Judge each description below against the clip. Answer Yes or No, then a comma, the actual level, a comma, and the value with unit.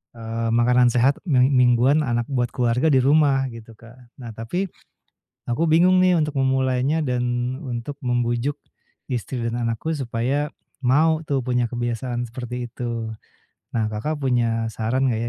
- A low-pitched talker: Yes, low, 125 Hz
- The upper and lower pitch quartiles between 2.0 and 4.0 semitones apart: Yes, narrow, 2.6 semitones